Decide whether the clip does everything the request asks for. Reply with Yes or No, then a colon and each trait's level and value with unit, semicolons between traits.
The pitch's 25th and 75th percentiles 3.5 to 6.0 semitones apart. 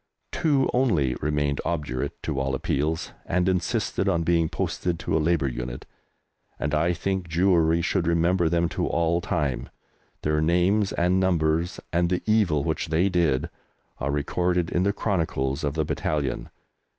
No: average, 3.1 semitones